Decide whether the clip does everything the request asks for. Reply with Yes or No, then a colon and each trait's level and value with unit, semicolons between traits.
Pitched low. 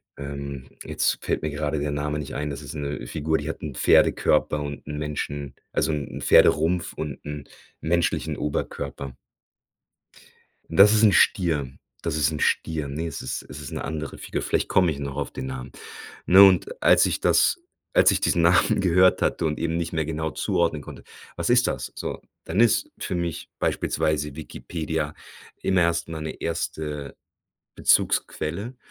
Yes: very low, 75 Hz